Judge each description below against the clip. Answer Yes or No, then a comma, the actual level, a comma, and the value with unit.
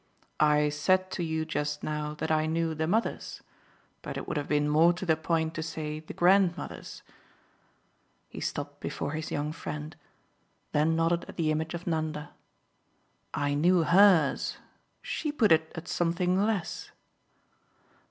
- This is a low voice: No, medium, 160 Hz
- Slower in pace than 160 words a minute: Yes, average, 150 wpm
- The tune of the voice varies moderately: No, narrow, 2.3 semitones